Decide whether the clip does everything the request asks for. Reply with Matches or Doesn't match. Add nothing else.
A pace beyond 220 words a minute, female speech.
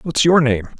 Doesn't match